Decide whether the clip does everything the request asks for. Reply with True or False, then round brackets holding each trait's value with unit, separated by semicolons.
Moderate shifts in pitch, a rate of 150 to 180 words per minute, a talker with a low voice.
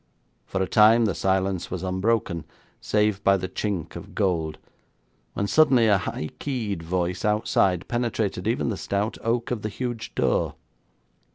True (3.5 semitones; 155 wpm; 100 Hz)